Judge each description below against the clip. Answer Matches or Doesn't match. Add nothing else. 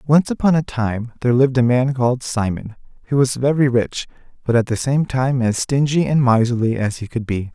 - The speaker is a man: Matches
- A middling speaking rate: Doesn't match